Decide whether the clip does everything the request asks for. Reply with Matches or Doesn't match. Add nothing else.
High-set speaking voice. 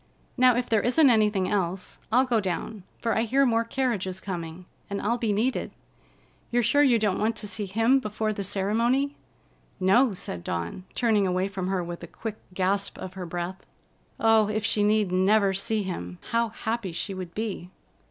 Matches